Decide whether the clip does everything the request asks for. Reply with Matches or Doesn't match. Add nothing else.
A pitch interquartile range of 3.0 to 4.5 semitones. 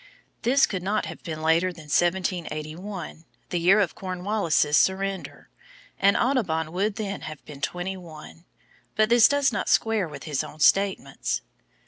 Matches